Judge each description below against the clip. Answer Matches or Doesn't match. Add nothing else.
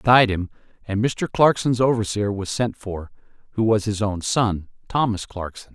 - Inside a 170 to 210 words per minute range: Matches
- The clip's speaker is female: Doesn't match